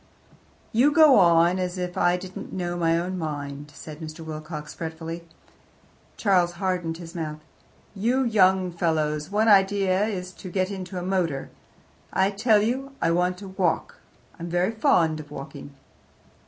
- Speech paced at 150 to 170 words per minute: Yes, average, 155 wpm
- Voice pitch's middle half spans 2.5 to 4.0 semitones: Yes, average, 2.9 semitones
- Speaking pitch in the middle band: Yes, medium, 180 Hz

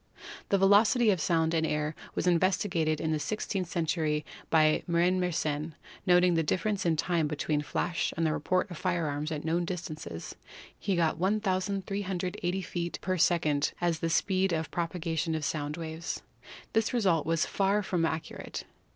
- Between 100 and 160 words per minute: No, average, 170 wpm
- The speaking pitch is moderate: Yes, medium, 170 Hz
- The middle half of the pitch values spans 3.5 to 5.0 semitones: No, average, 2.7 semitones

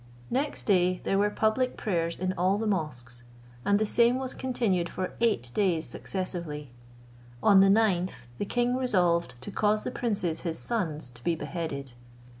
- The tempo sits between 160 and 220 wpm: Yes, average, 165 wpm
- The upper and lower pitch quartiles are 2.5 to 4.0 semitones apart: No, average, 4.7 semitones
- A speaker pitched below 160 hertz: No, medium, 185 Hz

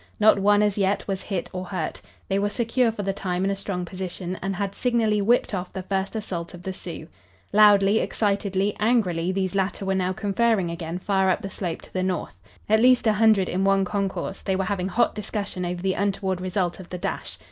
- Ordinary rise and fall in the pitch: No, narrow, 2.0 semitones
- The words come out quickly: Yes, fast, 220 wpm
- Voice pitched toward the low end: No, high, 195 Hz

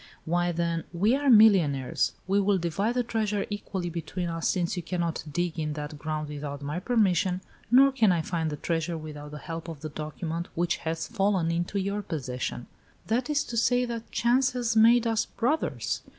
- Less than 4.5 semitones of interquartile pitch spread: No, wide, 5.5 semitones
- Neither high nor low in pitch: Yes, medium, 175 Hz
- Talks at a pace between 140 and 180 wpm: No, average, 190 wpm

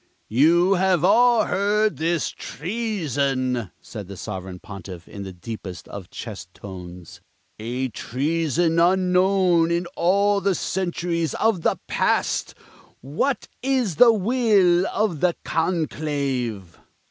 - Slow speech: Yes, slow, 115 wpm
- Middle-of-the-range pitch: Yes, medium, 165 Hz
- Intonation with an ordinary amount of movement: No, wide, 7.8 semitones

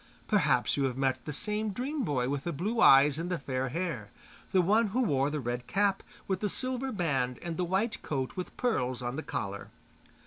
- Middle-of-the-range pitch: Yes, medium, 165 Hz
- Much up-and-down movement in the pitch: Yes, wide, 7.6 semitones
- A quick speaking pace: Yes, fast, 210 wpm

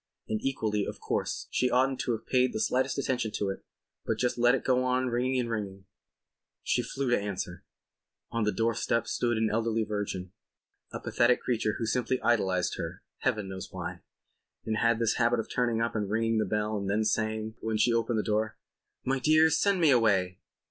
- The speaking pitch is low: Yes, low, 115 Hz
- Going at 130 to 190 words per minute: No, average, 200 wpm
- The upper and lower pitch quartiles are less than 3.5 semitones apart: Yes, average, 2.7 semitones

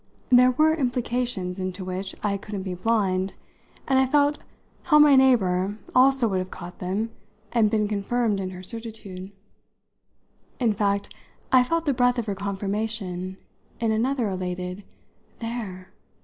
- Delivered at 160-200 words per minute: No, average, 150 wpm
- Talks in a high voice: Yes, high, 210 Hz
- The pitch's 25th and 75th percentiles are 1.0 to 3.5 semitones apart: No, average, 4.8 semitones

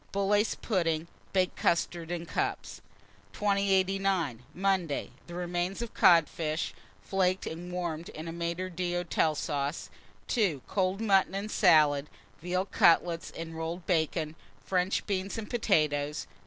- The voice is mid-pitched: Yes, medium, 175 Hz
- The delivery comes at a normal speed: No, slow, 130 wpm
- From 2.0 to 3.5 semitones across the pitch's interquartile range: Yes, average, 3.0 semitones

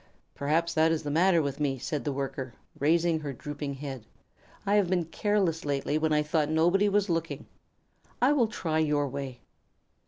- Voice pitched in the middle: Yes, medium, 155 Hz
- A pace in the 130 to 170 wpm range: No, average, 185 wpm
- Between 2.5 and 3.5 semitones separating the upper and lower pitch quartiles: Yes, average, 3.2 semitones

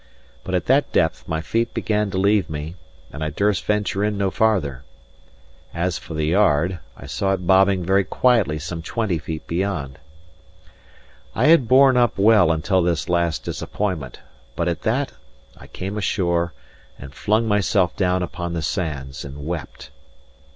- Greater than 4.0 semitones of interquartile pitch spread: Yes, average, 4.5 semitones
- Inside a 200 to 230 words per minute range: No, average, 160 wpm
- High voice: No, very low, 90 Hz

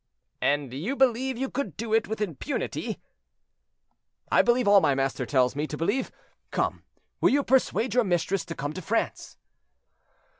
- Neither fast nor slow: Yes, average, 160 wpm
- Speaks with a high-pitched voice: Yes, high, 205 Hz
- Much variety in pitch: Yes, wide, 8.8 semitones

